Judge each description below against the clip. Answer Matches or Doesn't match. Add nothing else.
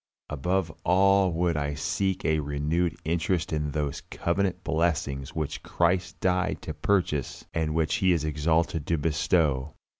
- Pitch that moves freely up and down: Doesn't match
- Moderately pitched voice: Doesn't match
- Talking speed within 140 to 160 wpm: Matches